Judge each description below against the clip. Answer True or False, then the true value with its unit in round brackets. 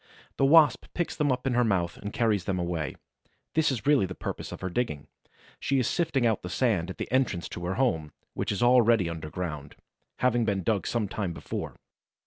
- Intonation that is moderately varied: False (6.3 semitones)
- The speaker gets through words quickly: True (210 wpm)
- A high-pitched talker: False (105 Hz)